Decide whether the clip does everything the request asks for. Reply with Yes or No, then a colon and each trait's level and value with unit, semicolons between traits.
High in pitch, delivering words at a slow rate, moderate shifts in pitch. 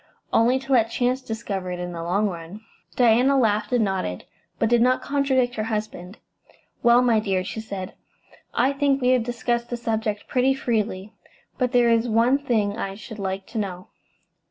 No: high, 225 Hz; average, 180 wpm; average, 3.6 semitones